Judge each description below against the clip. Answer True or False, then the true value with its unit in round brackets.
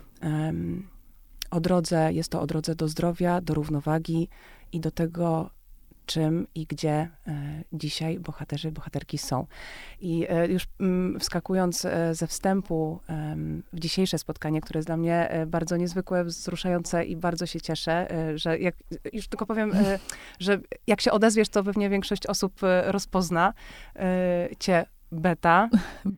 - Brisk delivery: False (130 wpm)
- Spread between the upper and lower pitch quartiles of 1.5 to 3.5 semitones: True (2.5 semitones)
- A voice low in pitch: False (170 Hz)